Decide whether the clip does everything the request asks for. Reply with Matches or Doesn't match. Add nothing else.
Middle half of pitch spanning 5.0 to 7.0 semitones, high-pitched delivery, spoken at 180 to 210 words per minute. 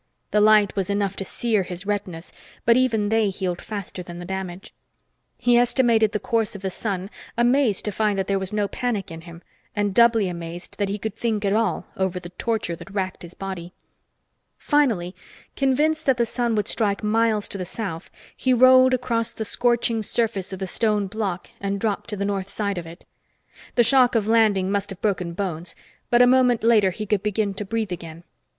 Doesn't match